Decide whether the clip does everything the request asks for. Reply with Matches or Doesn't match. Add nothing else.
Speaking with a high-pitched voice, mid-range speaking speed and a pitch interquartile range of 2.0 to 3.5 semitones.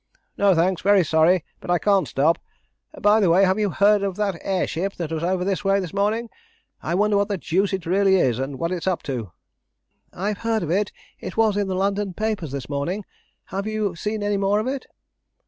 Doesn't match